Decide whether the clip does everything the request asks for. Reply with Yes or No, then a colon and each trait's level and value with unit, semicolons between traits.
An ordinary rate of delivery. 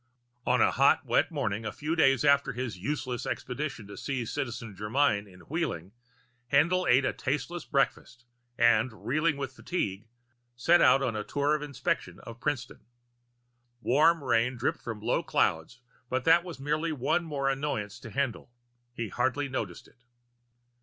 Yes: average, 160 wpm